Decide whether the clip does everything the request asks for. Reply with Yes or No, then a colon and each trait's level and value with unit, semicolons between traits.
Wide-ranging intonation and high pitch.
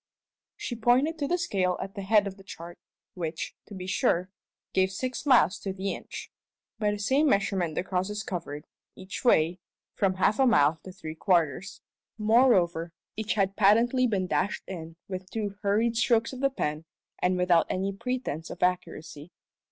No: average, 3.8 semitones; high, 195 Hz